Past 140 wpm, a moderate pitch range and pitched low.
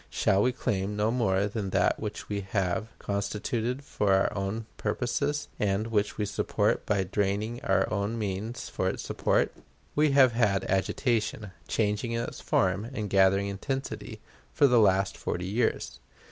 Yes: average, 160 wpm; average, 3.0 semitones; low, 105 Hz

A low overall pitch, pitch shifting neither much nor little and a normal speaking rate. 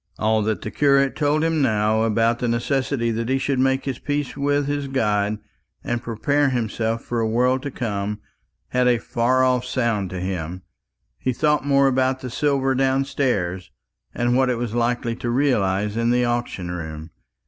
Yes: low, 120 Hz; average, 3.4 semitones; average, 180 wpm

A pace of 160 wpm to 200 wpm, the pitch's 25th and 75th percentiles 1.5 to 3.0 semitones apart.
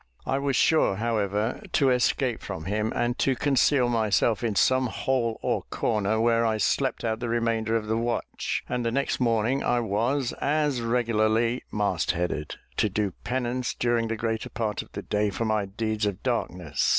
Yes: average, 180 wpm; narrow, 2.4 semitones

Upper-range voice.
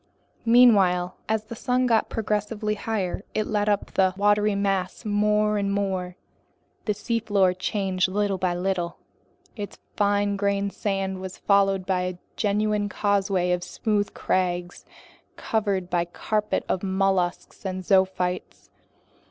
Yes: high, 200 Hz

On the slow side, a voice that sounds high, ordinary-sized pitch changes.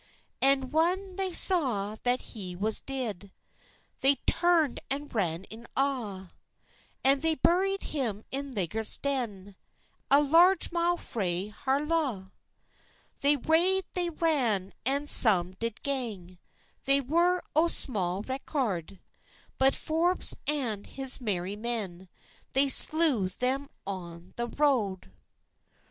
No: slow, 115 wpm; very high, 265 Hz; wide, 7.2 semitones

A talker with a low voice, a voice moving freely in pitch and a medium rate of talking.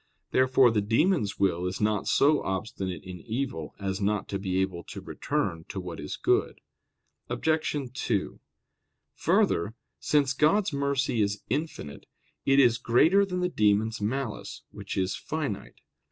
Yes: low, 110 Hz; wide, 6.4 semitones; average, 145 wpm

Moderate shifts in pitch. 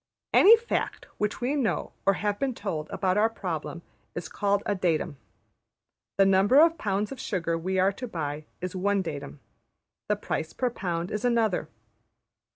Yes: average, 4.3 semitones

